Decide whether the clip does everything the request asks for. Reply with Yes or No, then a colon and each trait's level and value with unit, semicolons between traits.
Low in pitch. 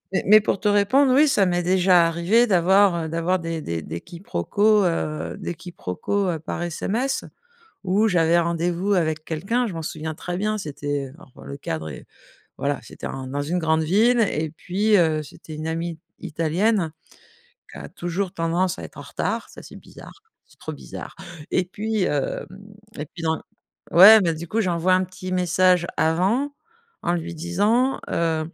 No: medium, 175 Hz